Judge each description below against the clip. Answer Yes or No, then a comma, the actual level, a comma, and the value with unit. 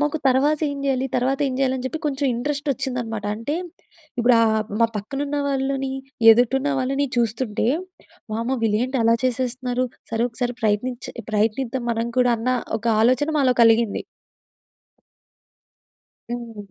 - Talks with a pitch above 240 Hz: Yes, very high, 250 Hz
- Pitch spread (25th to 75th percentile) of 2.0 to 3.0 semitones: Yes, average, 2.7 semitones